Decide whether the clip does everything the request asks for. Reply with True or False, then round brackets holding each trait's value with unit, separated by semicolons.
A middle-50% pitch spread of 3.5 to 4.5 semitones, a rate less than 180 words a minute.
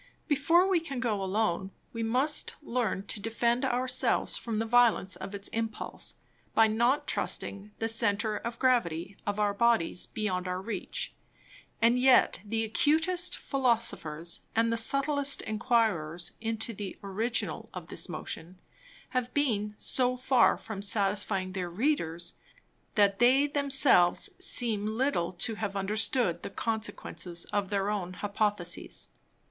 True (4.1 semitones; 140 wpm)